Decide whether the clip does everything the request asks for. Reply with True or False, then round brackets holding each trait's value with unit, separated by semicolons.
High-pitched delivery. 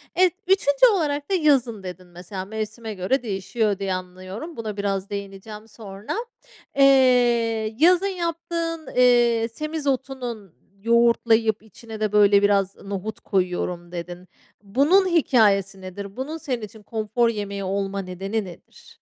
True (220 Hz)